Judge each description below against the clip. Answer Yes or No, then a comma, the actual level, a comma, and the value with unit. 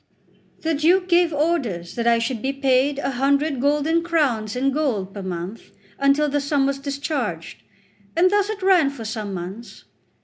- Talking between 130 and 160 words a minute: No, average, 170 wpm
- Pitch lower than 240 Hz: No, very high, 275 Hz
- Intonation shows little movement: No, average, 5.1 semitones